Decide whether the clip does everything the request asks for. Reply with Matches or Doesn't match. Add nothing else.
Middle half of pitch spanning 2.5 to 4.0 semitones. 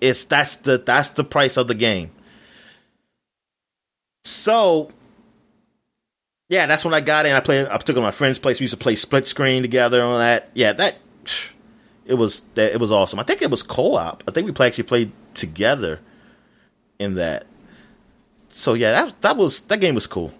Matches